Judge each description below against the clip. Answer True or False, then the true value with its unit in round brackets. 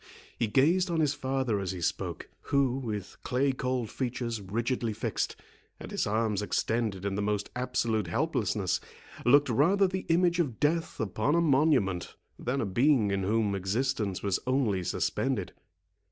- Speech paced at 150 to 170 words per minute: True (155 wpm)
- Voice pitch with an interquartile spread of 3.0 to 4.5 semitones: False (5.2 semitones)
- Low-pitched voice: True (120 Hz)